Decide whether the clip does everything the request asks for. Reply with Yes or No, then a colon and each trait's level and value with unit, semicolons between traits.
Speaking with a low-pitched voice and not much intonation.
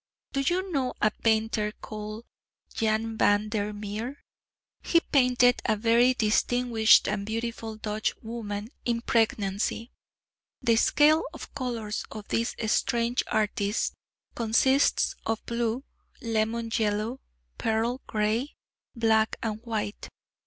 No: high, 225 Hz; narrow, 2.0 semitones